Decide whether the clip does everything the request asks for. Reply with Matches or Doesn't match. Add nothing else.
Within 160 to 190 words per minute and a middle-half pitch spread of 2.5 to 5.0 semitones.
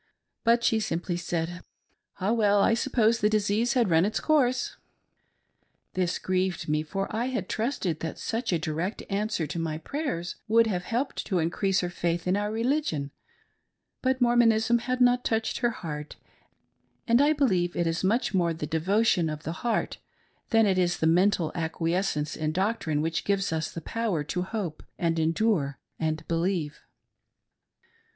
Doesn't match